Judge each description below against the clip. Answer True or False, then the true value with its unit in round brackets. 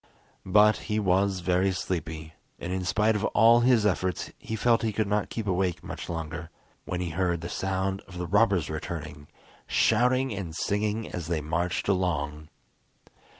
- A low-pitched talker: True (95 Hz)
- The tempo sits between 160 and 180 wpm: True (165 wpm)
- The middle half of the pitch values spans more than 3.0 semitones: True (3.7 semitones)